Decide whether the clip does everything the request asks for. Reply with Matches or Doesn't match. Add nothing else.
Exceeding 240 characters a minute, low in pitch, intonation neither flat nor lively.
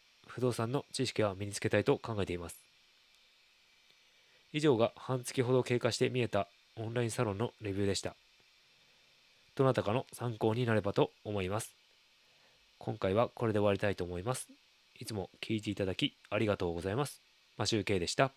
Matches